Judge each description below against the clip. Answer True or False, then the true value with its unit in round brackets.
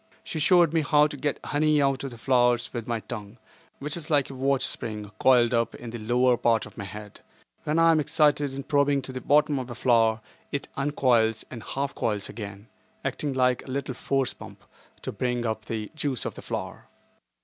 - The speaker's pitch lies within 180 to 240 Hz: False (130 Hz)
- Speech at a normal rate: False (210 wpm)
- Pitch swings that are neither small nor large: True (3.8 semitones)